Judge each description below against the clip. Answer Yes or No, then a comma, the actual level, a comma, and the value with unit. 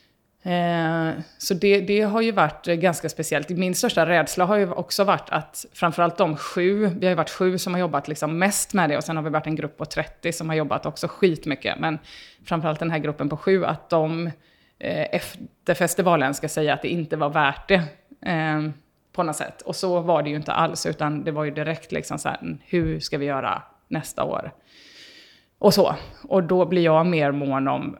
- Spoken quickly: Yes, fast, 210 wpm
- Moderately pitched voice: Yes, medium, 165 Hz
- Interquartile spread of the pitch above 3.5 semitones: No, average, 2.9 semitones